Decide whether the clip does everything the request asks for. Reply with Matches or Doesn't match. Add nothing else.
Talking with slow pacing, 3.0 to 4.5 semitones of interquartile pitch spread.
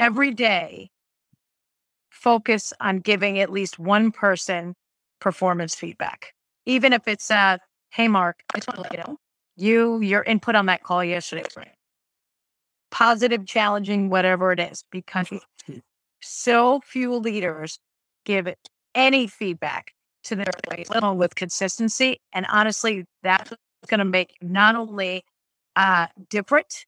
Matches